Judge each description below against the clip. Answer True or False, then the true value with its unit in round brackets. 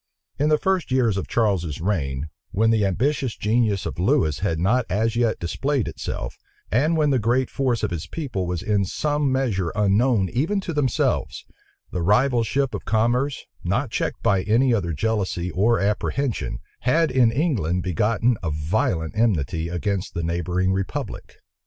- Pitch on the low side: True (110 Hz)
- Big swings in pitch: True (5.9 semitones)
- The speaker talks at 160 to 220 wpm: True (165 wpm)